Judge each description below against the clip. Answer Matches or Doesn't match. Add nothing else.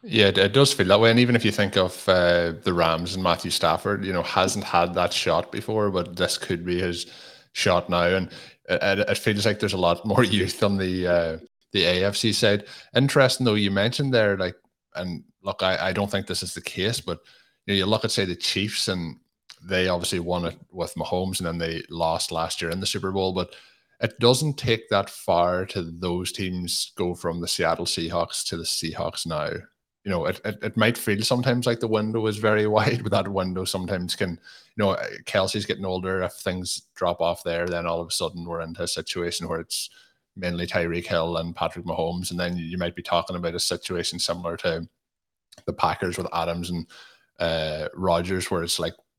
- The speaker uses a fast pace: Matches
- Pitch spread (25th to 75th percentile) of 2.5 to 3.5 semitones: Matches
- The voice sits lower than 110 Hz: Matches